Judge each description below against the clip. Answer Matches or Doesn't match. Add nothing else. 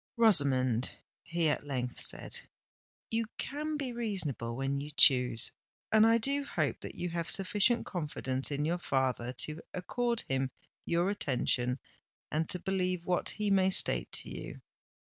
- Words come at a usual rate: Matches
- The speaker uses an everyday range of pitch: Doesn't match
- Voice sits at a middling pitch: Matches